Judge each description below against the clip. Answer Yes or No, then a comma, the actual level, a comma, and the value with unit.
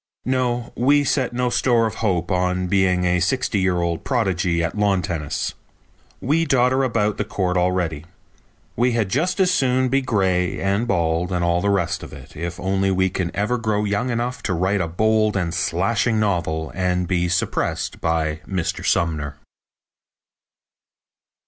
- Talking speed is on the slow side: No, average, 165 wpm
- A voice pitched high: No, very low, 95 Hz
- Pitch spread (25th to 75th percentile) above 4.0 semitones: Yes, average, 5.1 semitones